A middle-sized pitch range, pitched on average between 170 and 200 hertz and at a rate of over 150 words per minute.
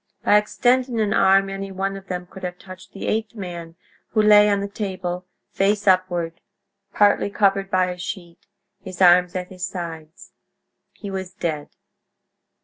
No: narrow, 2.1 semitones; high, 190 Hz; average, 160 wpm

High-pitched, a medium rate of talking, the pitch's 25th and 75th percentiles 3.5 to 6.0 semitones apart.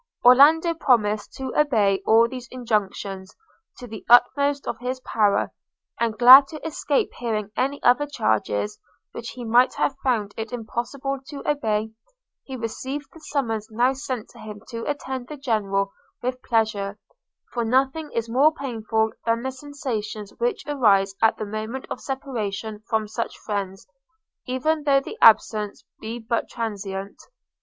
Yes: high, 235 Hz; average, 150 wpm; average, 3.9 semitones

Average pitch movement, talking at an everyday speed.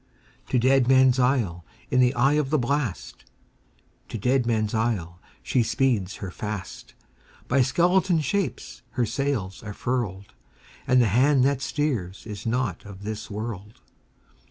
No: average, 4.3 semitones; slow, 125 wpm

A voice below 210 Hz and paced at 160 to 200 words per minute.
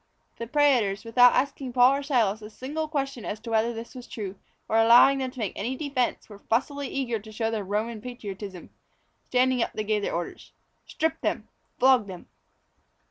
No: high, 235 Hz; average, 190 wpm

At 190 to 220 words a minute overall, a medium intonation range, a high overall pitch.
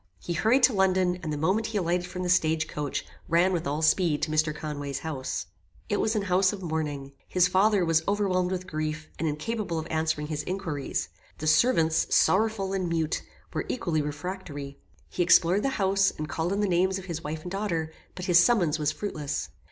No: average, 200 wpm; average, 3.7 semitones; medium, 175 Hz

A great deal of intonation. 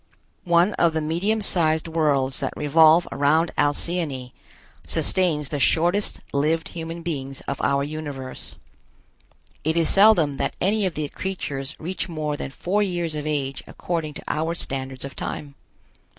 No: average, 3.2 semitones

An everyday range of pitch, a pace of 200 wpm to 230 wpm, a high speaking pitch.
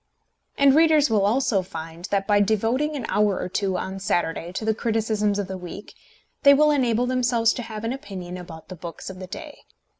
Yes: average, 4.7 semitones; fast, 205 wpm; high, 210 Hz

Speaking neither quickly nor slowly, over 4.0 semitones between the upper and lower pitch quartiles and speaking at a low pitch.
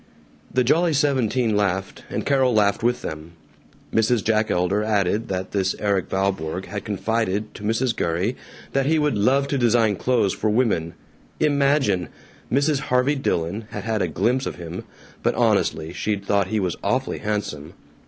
Yes: average, 165 wpm; average, 4.8 semitones; low, 105 Hz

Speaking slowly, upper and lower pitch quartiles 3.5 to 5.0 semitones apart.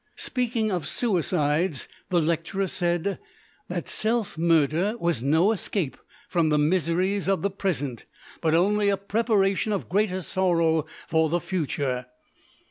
Yes: slow, 130 wpm; average, 3.8 semitones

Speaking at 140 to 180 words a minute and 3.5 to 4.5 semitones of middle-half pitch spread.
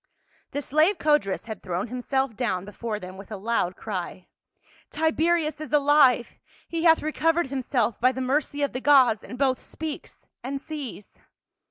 No: average, 165 wpm; wide, 5.4 semitones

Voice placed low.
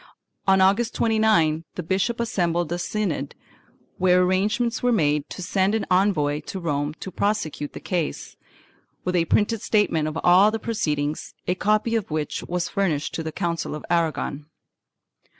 No: medium, 180 Hz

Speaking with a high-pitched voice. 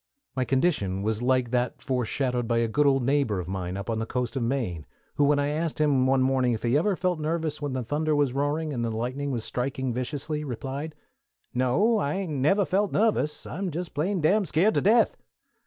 No: medium, 140 Hz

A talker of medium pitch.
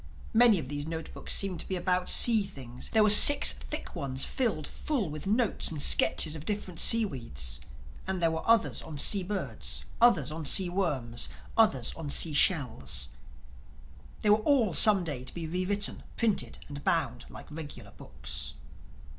Yes: medium, 170 Hz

